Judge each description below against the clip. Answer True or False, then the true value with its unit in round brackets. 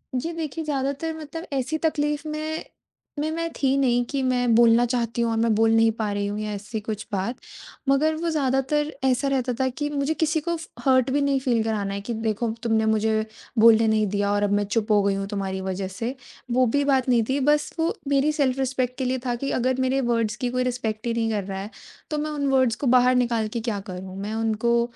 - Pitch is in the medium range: False (245 Hz)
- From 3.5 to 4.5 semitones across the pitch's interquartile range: True (4.1 semitones)